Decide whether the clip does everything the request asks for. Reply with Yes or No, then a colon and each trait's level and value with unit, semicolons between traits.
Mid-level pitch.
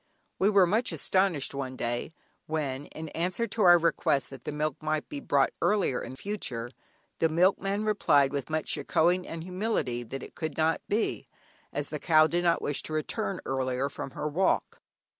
Yes: medium, 160 Hz